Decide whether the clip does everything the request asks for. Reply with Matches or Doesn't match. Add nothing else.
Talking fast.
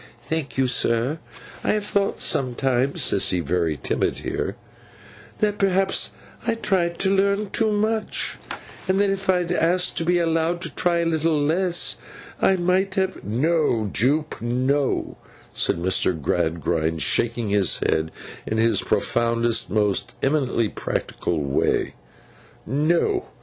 Doesn't match